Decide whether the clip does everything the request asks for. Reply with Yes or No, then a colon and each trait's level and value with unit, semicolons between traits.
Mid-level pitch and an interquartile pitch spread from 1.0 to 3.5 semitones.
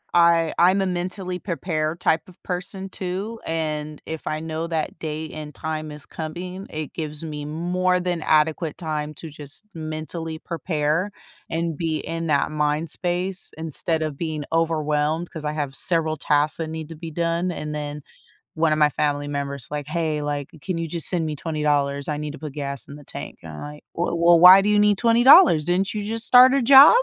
Yes: medium, 160 Hz; narrow, 2.6 semitones